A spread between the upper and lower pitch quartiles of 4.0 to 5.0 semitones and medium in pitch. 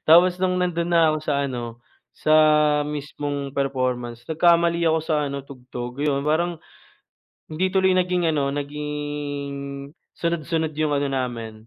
No: average, 3.4 semitones; medium, 150 Hz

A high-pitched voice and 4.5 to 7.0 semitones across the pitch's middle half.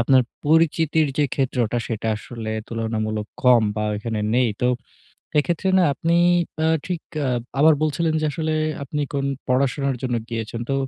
No: low, 130 Hz; average, 5.2 semitones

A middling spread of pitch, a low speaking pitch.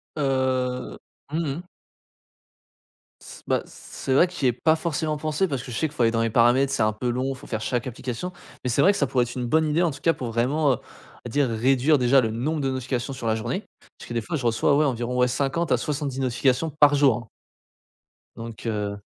Yes: average, 3.5 semitones; low, 130 Hz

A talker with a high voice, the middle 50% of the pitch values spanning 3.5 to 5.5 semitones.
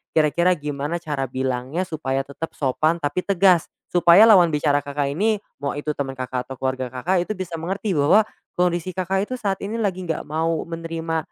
No: medium, 165 Hz; average, 4.2 semitones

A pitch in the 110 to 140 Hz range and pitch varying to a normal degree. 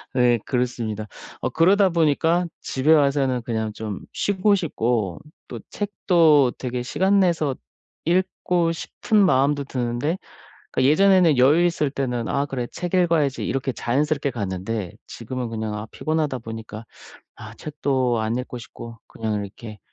No: low, 135 Hz; wide, 6.0 semitones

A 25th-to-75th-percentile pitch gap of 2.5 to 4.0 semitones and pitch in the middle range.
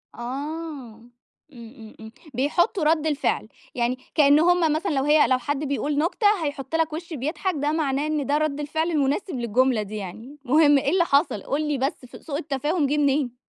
No: average, 2.8 semitones; very high, 290 Hz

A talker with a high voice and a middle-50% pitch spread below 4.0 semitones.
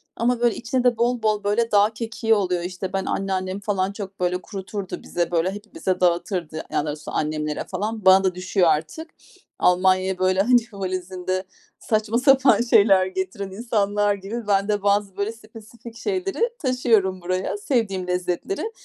Yes: high, 200 Hz; average, 3.2 semitones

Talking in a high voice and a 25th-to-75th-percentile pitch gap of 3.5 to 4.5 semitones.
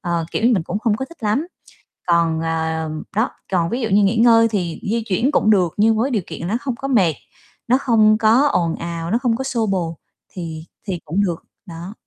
No: high, 205 Hz; wide, 5.5 semitones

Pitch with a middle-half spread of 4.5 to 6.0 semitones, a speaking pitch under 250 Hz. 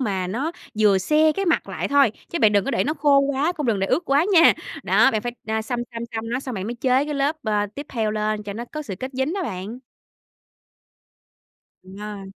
Yes: average, 5.2 semitones; high, 240 Hz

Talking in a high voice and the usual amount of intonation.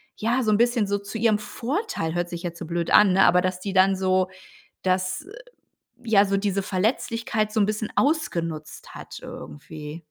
Yes: high, 195 Hz; average, 3.4 semitones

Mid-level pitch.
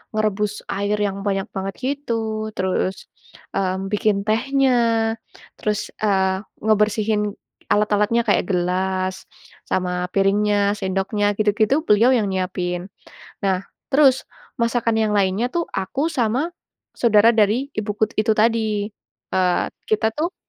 No: high, 210 Hz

